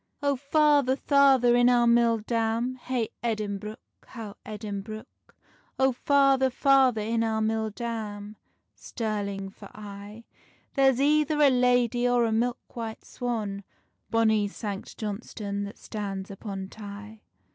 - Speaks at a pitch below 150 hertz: No, high, 225 Hz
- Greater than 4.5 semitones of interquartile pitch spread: No, average, 3.1 semitones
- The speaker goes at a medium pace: No, slow, 125 wpm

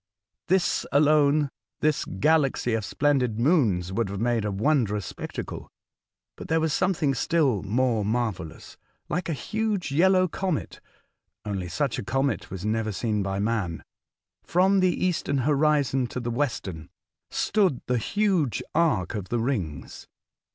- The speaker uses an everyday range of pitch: No, wide, 6.9 semitones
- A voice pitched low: Yes, low, 130 Hz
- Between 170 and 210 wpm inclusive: No, average, 150 wpm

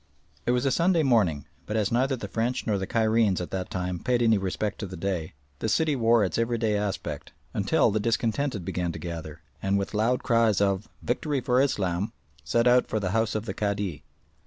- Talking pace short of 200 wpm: No, fast, 205 wpm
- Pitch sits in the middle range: No, low, 110 Hz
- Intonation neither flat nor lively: Yes, average, 3.8 semitones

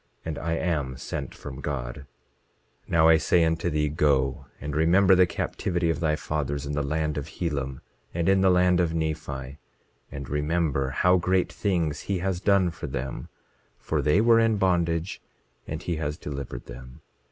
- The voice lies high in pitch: No, very low, 80 Hz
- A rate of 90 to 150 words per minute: No, average, 175 wpm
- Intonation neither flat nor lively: Yes, average, 3.5 semitones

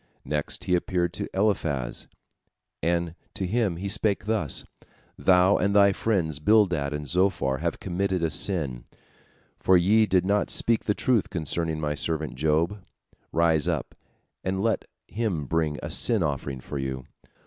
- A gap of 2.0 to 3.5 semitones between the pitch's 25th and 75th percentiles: No, average, 4.8 semitones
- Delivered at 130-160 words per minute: Yes, average, 150 wpm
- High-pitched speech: No, very low, 85 Hz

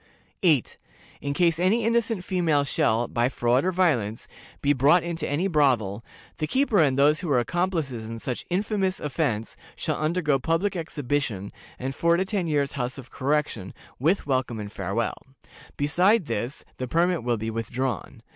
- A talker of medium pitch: Yes, medium, 145 Hz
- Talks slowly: No, average, 165 wpm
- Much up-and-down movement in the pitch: Yes, wide, 6.3 semitones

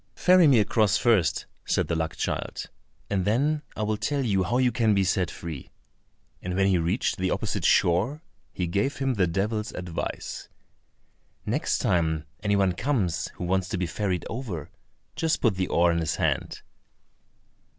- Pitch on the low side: Yes, very low, 95 Hz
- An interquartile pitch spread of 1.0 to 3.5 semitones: No, average, 4.5 semitones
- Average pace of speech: Yes, average, 170 wpm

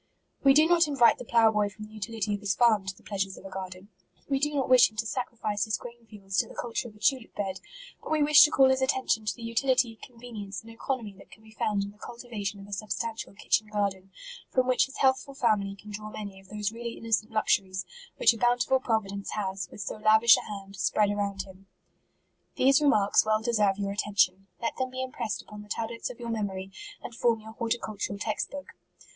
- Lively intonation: No, average, 3.1 semitones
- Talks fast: Yes, fast, 235 wpm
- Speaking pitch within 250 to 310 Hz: No, high, 215 Hz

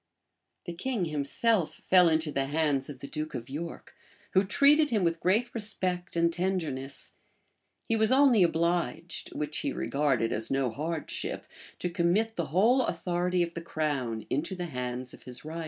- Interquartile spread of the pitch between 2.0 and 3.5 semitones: No, average, 4.4 semitones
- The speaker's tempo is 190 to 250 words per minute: No, average, 170 wpm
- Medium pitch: Yes, medium, 170 Hz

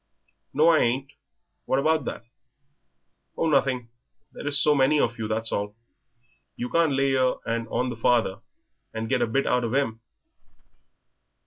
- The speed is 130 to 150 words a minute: No, average, 160 wpm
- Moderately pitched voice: No, low, 130 Hz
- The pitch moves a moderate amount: Yes, average, 3.5 semitones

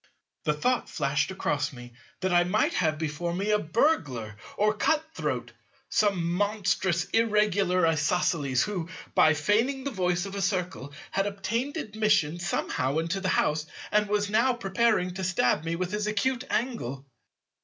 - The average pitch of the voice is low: No, medium, 185 Hz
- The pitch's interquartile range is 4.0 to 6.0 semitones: Yes, average, 4.7 semitones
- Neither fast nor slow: Yes, average, 155 wpm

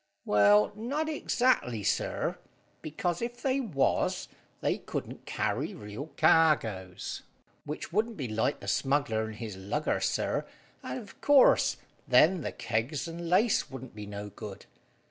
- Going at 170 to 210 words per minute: No, average, 140 wpm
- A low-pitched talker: No, medium, 145 Hz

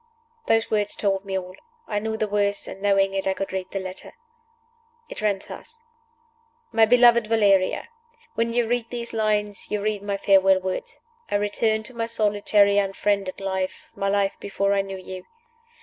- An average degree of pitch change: No, narrow, 2.0 semitones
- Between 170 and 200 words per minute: Yes, average, 175 wpm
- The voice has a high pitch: Yes, high, 205 Hz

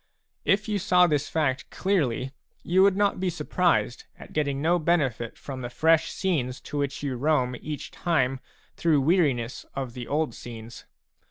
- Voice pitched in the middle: Yes, medium, 145 Hz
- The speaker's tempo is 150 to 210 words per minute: Yes, average, 165 wpm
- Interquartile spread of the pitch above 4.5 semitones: Yes, average, 5.3 semitones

